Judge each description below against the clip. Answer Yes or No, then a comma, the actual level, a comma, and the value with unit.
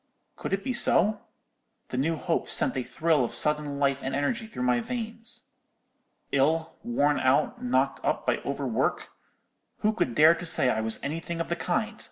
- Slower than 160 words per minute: No, average, 185 wpm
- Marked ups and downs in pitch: Yes, wide, 7.7 semitones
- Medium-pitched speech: Yes, medium, 160 Hz